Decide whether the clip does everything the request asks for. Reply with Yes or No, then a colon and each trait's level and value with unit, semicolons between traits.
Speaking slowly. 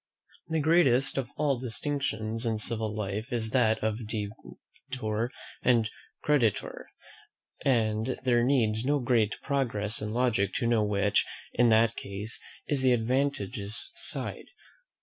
Yes: slow, 130 wpm